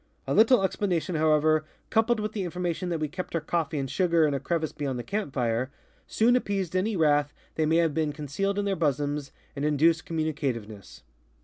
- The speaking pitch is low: No, medium, 160 Hz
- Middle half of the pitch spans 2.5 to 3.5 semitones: No, average, 4.1 semitones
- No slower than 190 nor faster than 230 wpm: Yes, average, 195 wpm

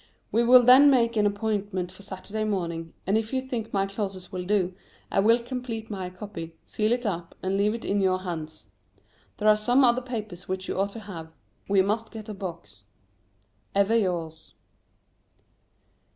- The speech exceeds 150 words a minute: Yes, average, 180 wpm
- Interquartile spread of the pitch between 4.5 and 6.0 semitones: No, average, 3.3 semitones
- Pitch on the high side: Yes, high, 205 Hz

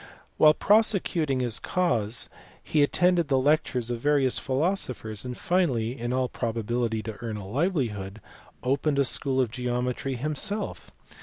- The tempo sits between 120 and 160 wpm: Yes, average, 140 wpm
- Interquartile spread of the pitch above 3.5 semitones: Yes, average, 4.5 semitones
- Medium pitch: No, low, 130 Hz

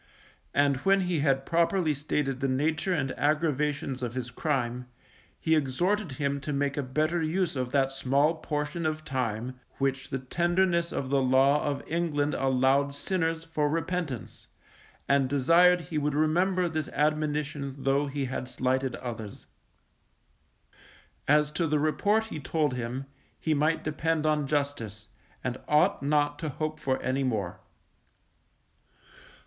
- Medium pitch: Yes, medium, 145 Hz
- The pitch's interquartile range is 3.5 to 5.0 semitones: No, average, 3.1 semitones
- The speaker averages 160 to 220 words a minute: No, average, 145 wpm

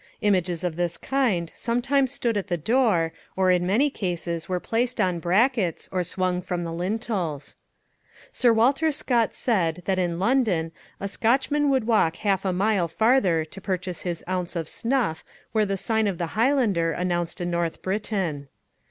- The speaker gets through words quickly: No, average, 170 wpm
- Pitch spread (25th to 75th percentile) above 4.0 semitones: Yes, average, 5.0 semitones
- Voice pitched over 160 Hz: Yes, high, 190 Hz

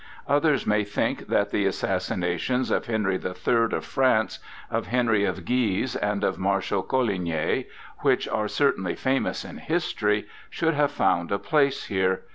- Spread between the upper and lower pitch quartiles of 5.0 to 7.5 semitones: Yes, average, 5.3 semitones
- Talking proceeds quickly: No, average, 155 wpm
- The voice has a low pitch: Yes, low, 105 Hz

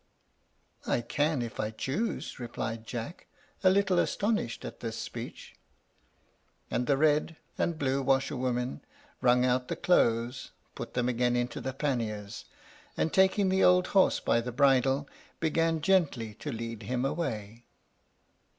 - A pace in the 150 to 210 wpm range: No, average, 140 wpm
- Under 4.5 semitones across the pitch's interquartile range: No, average, 5.1 semitones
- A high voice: No, low, 130 Hz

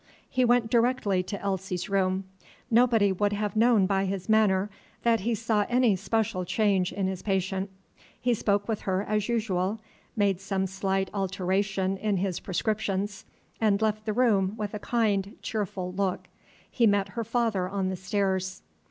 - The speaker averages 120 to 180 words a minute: Yes, average, 160 wpm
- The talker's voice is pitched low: No, high, 200 Hz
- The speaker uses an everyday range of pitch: No, narrow, 2.3 semitones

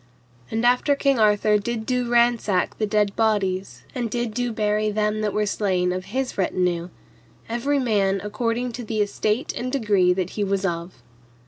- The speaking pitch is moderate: No, high, 215 Hz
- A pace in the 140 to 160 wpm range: No, average, 175 wpm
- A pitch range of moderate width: Yes, average, 3.3 semitones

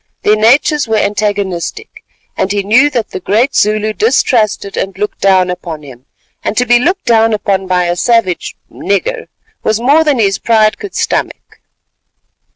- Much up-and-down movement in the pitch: No, average, 4.0 semitones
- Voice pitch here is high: Yes, high, 215 Hz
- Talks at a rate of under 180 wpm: Yes, average, 160 wpm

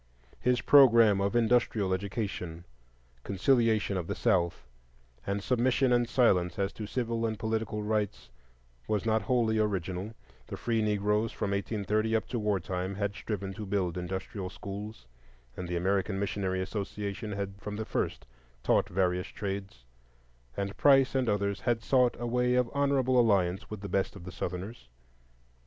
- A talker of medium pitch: No, low, 105 Hz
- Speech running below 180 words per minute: Yes, average, 155 wpm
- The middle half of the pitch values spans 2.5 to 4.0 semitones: Yes, average, 3.0 semitones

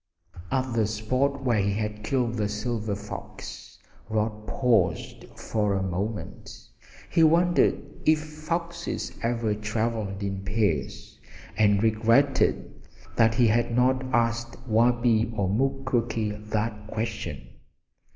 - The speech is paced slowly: Yes, slow, 115 wpm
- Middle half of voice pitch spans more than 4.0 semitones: No, average, 3.0 semitones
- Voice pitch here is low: Yes, low, 115 Hz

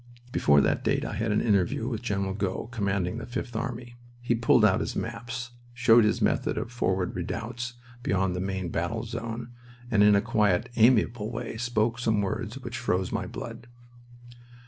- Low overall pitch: Yes, low, 115 Hz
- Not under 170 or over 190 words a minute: Yes, average, 175 wpm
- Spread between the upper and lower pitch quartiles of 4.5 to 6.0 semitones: No, average, 3.3 semitones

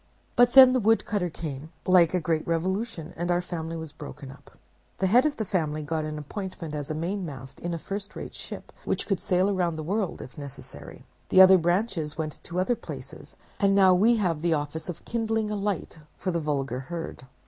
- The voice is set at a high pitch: No, medium, 175 Hz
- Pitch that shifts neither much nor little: Yes, average, 4.3 semitones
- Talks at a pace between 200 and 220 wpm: Yes, fast, 205 wpm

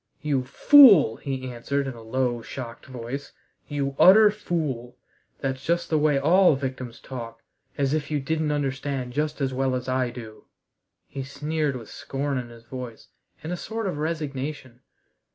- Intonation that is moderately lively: Yes, average, 3.1 semitones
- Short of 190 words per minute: Yes, average, 165 wpm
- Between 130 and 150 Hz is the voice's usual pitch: Yes, low, 135 Hz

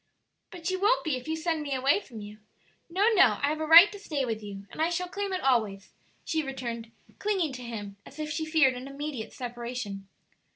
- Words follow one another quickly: Yes, fast, 220 wpm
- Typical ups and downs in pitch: No, wide, 5.8 semitones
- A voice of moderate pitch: No, very high, 280 Hz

